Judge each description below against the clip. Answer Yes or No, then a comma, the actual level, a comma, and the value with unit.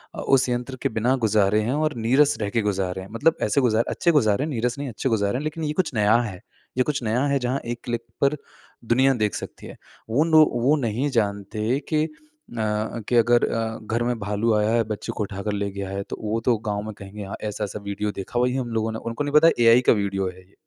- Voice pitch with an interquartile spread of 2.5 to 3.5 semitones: No, average, 4.1 semitones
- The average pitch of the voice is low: Yes, low, 115 Hz